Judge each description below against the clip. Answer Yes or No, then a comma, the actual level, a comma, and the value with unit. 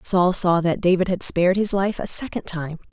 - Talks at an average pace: No, fast, 225 wpm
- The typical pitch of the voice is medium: Yes, medium, 180 Hz